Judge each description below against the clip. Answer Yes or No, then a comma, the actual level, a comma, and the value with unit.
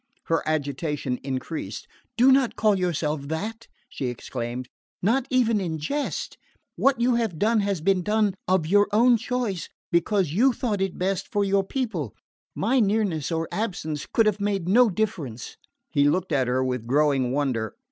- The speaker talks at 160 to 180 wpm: Yes, average, 165 wpm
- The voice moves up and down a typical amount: No, wide, 6.8 semitones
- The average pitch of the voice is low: No, medium, 185 Hz